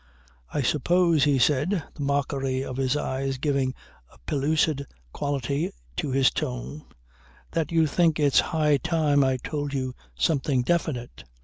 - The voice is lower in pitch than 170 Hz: Yes, medium, 140 Hz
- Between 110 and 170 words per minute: Yes, average, 140 wpm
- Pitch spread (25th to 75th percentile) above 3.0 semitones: No, average, 2.7 semitones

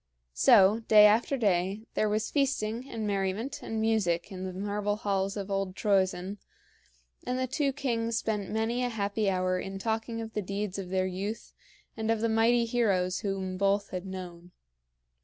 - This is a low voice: No, high, 205 Hz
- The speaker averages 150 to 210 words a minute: Yes, average, 175 wpm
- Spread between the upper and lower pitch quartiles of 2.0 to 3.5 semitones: Yes, average, 2.8 semitones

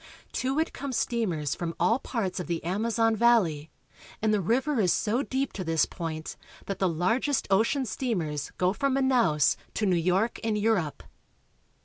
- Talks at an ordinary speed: Yes, average, 170 wpm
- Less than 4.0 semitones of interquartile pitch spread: No, wide, 5.6 semitones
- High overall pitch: Yes, high, 210 Hz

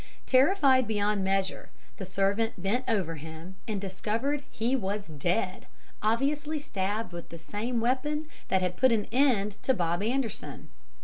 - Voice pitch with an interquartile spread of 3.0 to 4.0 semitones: No, average, 5.2 semitones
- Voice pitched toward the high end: Yes, high, 210 Hz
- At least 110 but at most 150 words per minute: Yes, average, 145 wpm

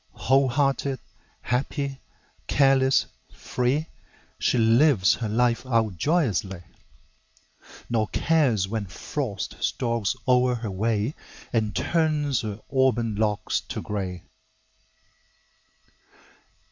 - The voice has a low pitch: Yes, low, 120 Hz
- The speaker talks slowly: Yes, slow, 95 wpm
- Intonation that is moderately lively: Yes, average, 4.3 semitones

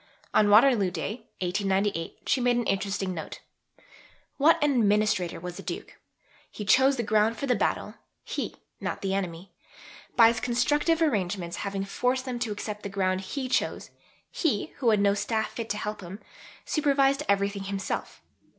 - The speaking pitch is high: Yes, high, 210 Hz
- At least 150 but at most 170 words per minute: Yes, average, 165 wpm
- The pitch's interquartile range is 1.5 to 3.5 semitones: No, average, 4.0 semitones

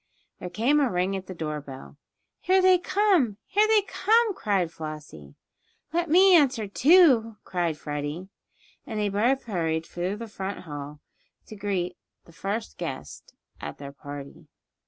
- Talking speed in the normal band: Yes, average, 155 wpm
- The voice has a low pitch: No, high, 195 Hz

